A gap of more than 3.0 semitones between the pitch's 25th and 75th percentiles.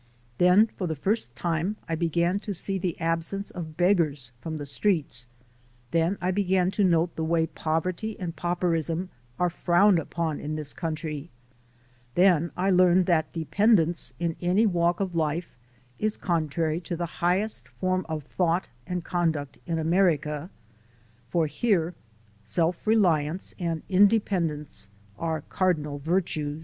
No: narrow, 2.6 semitones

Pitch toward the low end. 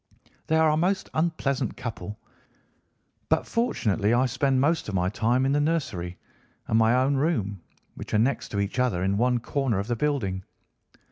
Yes: low, 125 Hz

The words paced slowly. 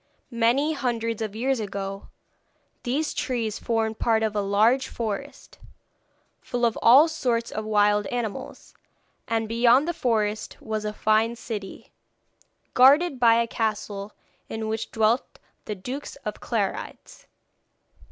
Yes: slow, 130 wpm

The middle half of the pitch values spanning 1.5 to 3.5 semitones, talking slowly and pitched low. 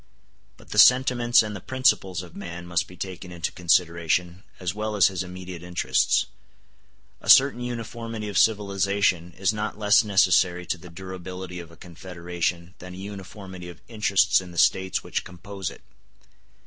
No: average, 2.8 semitones; average, 160 wpm; very low, 95 Hz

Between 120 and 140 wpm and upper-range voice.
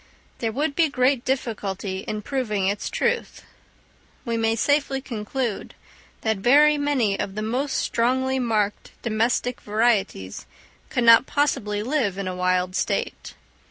Yes: slow, 135 wpm; high, 230 Hz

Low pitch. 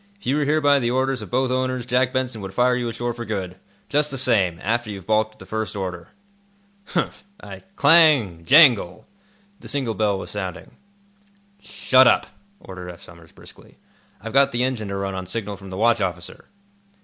Yes: low, 115 Hz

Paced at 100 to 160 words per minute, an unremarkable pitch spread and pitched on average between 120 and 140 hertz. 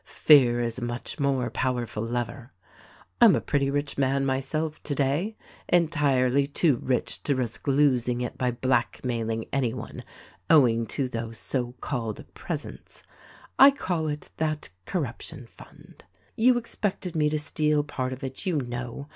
Yes: average, 155 wpm; average, 3.7 semitones; low, 135 Hz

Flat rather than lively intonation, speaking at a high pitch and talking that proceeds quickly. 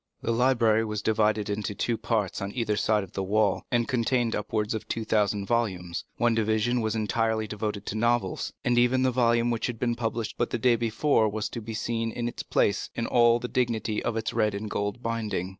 No: narrow, 1.9 semitones; low, 110 Hz; fast, 215 wpm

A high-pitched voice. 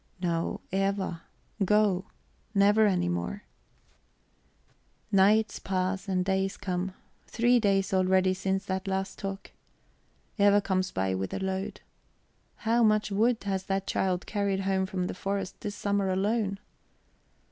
Yes: high, 195 Hz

